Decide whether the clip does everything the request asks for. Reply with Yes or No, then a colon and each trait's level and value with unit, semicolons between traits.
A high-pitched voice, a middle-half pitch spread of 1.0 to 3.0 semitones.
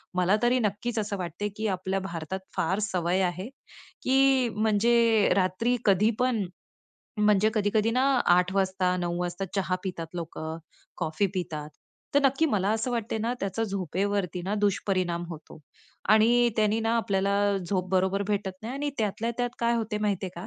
No: high, 200 Hz; average, 3.4 semitones